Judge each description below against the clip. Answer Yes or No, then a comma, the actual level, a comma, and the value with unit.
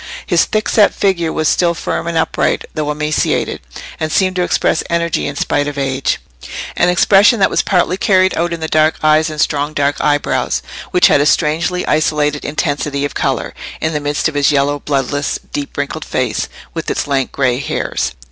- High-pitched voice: No, medium, 155 Hz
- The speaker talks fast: No, average, 185 wpm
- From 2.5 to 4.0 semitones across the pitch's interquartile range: Yes, average, 2.9 semitones